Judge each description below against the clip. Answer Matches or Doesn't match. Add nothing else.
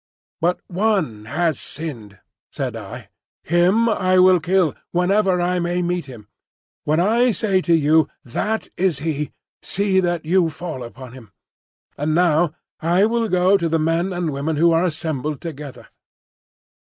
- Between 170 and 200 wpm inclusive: Doesn't match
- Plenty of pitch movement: Doesn't match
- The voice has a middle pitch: Matches